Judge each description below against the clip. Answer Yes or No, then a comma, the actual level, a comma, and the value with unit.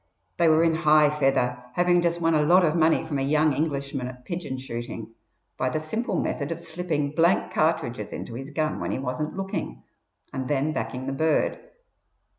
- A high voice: No, medium, 150 Hz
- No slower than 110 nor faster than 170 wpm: No, average, 190 wpm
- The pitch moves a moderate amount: Yes, average, 3.6 semitones